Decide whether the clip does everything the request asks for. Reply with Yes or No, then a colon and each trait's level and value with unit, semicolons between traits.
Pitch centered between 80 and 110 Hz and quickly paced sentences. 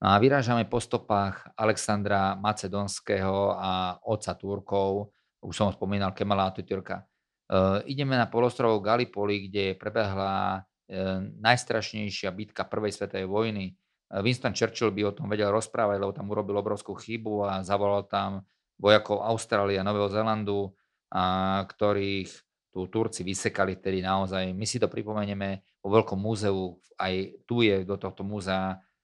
No: low, 100 Hz; average, 140 wpm